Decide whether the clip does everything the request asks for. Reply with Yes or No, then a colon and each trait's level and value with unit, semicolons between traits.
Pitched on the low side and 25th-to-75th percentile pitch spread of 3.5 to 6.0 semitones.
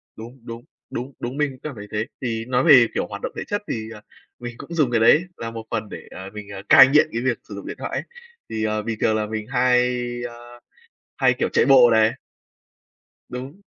No: low, 120 Hz; average, 2.7 semitones